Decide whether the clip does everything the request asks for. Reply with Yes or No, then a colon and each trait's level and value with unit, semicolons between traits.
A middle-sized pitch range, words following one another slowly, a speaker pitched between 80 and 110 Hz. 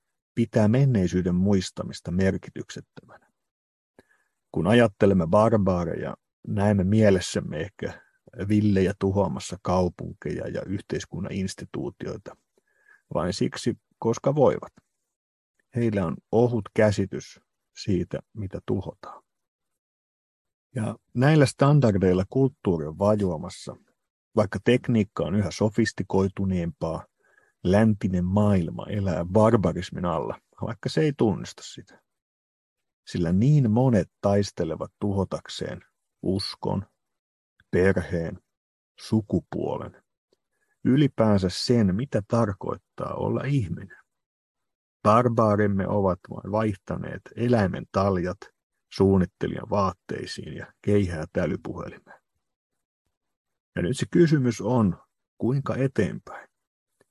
Yes: average, 3.6 semitones; slow, 85 wpm; low, 100 Hz